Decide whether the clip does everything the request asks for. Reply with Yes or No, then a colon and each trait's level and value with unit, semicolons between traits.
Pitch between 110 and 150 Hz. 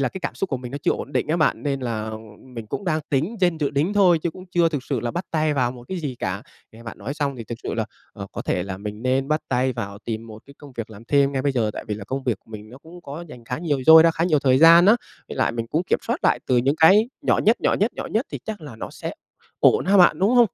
Yes: medium, 140 Hz